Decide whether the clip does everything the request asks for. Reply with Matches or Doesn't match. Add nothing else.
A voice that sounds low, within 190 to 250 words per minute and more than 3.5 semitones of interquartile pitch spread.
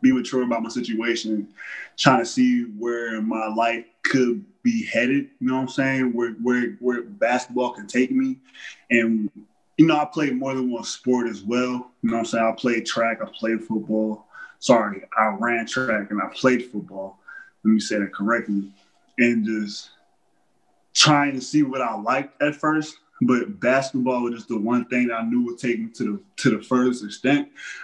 Doesn't match